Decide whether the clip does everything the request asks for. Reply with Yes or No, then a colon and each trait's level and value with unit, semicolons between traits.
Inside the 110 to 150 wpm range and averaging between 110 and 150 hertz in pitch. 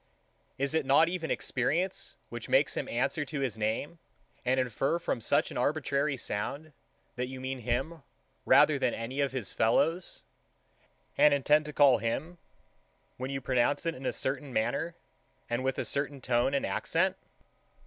No: average, 165 wpm; low, 135 Hz